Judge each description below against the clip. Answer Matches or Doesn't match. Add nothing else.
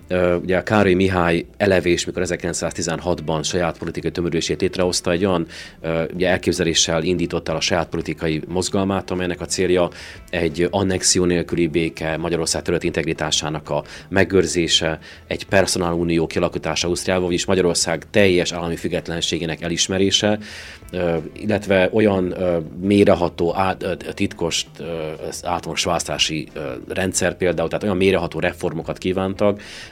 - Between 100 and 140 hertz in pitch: Doesn't match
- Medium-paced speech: Matches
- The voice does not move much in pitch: Matches